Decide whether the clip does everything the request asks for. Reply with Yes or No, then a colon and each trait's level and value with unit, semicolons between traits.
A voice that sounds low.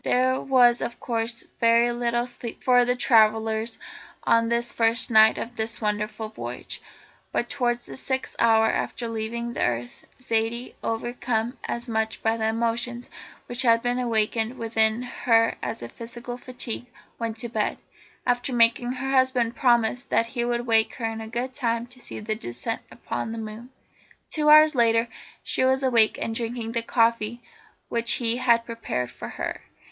No: high, 235 Hz